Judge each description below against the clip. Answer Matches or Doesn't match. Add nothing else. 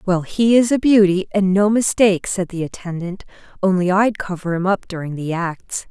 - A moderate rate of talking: Matches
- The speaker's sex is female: Matches